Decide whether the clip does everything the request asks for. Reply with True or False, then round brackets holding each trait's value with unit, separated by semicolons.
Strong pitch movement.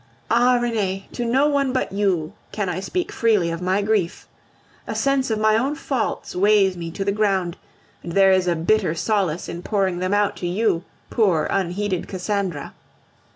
False (3.5 semitones)